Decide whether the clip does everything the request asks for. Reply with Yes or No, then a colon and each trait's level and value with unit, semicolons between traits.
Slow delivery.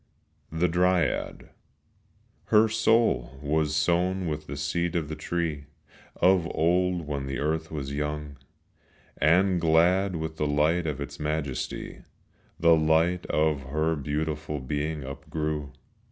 Yes: slow, 125 wpm